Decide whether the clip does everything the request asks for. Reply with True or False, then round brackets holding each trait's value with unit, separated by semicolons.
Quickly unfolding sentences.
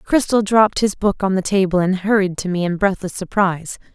True (215 wpm)